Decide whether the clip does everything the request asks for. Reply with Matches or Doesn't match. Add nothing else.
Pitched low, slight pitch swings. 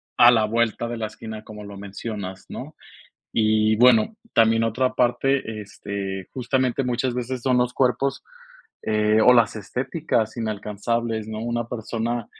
Matches